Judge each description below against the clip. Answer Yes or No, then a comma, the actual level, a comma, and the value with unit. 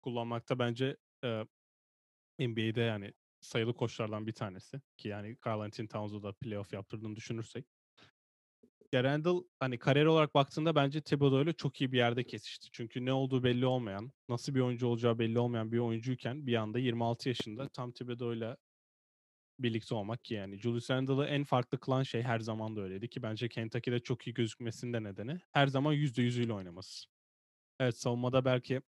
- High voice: No, low, 120 Hz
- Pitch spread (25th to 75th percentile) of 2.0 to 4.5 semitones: Yes, average, 2.7 semitones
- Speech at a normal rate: No, fast, 160 wpm